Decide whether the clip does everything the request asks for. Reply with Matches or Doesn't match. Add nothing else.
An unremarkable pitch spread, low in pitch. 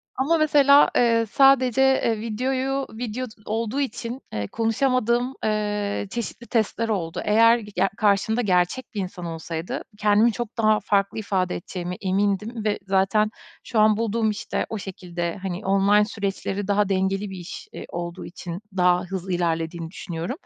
Doesn't match